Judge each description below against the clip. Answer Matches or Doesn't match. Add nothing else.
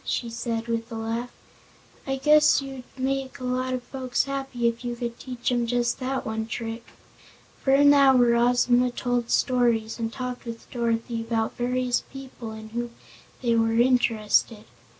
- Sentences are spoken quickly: Doesn't match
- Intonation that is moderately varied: Doesn't match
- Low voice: Doesn't match